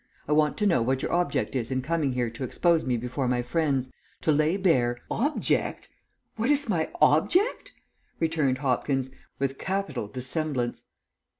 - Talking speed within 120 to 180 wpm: Yes, average, 165 wpm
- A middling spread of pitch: Yes, average, 4.8 semitones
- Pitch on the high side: No, medium, 145 Hz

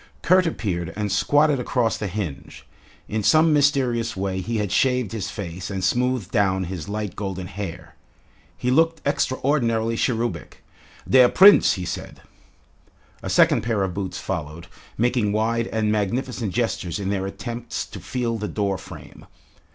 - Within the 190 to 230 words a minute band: No, average, 150 wpm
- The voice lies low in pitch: Yes, low, 110 Hz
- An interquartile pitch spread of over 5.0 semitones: No, average, 4.4 semitones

